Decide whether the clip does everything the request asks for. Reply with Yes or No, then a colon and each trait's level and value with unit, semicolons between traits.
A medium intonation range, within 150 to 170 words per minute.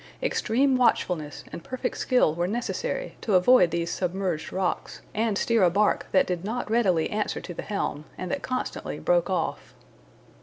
No: wide, 5.8 semitones; average, 165 wpm